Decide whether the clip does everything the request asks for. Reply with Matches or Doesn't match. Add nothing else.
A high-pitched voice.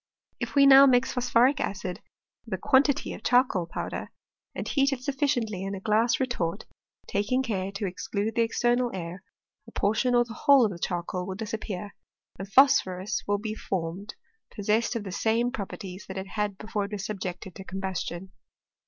Matches